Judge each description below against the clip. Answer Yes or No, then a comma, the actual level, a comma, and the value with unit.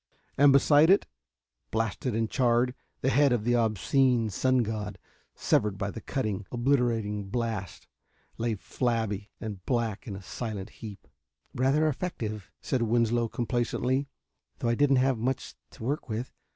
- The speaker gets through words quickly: No, average, 145 wpm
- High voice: No, low, 115 Hz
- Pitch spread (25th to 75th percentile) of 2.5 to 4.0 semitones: Yes, average, 3.3 semitones